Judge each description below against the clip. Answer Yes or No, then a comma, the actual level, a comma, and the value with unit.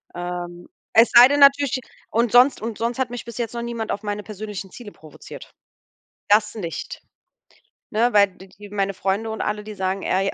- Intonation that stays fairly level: No, average, 3.3 semitones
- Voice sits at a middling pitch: No, high, 215 Hz